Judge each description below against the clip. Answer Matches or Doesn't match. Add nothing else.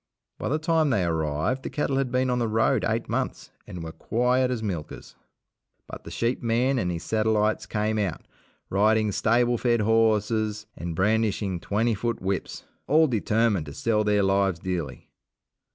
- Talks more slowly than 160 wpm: Doesn't match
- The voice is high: Doesn't match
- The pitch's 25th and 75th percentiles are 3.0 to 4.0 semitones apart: Matches